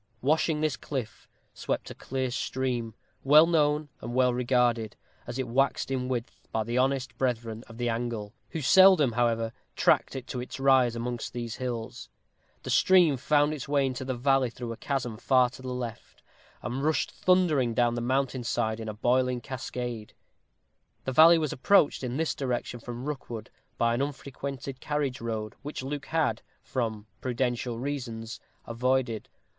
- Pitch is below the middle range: Yes, low, 125 Hz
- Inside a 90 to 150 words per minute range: No, average, 165 wpm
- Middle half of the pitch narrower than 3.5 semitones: Yes, average, 2.7 semitones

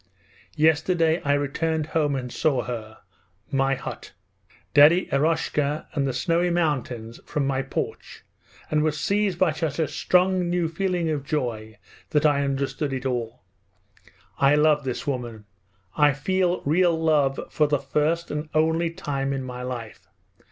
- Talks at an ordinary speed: Yes, average, 150 wpm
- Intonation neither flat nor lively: Yes, average, 3.3 semitones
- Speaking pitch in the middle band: Yes, medium, 150 Hz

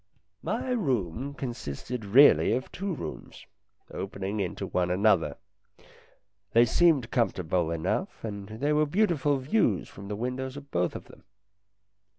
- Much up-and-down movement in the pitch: Yes, wide, 6.7 semitones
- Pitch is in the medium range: No, low, 115 Hz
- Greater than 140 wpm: No, slow, 135 wpm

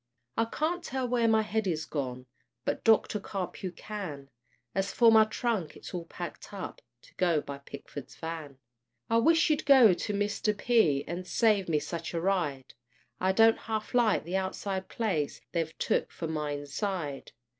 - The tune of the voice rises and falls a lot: Yes, wide, 5.8 semitones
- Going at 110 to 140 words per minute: No, average, 170 wpm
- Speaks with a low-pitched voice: No, high, 190 Hz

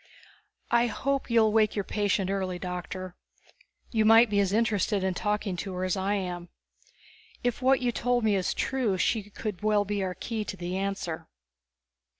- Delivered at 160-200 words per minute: Yes, average, 175 wpm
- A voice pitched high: Yes, high, 205 Hz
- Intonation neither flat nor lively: Yes, average, 3.1 semitones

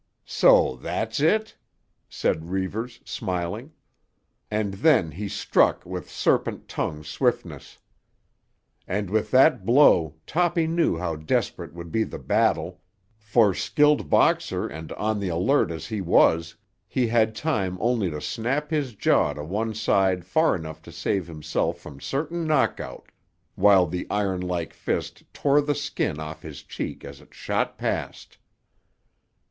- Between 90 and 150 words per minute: Yes, average, 140 wpm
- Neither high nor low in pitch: No, low, 105 Hz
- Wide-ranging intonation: Yes, wide, 7.8 semitones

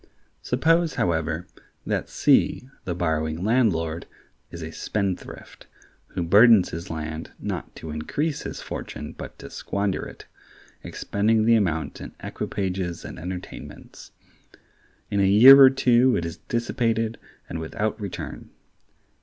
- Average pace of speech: No, slow, 130 wpm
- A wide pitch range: Yes, wide, 5.8 semitones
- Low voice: Yes, very low, 95 Hz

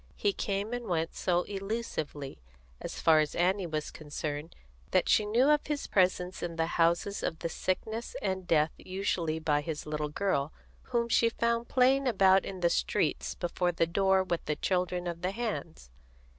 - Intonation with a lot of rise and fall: No, average, 4.3 semitones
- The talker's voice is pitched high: No, medium, 180 Hz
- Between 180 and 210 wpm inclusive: No, average, 170 wpm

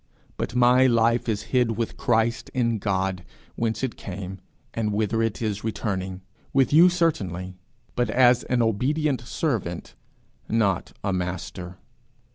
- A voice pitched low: Yes, low, 115 Hz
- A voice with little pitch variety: No, average, 4.2 semitones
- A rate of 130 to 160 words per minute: Yes, slow, 135 wpm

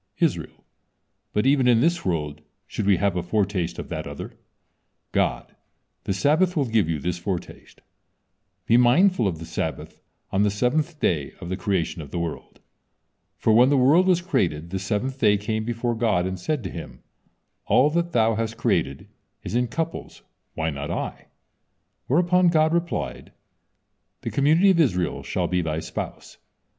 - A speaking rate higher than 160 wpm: Yes, average, 170 wpm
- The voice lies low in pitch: Yes, low, 110 Hz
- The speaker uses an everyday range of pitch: No, wide, 8.5 semitones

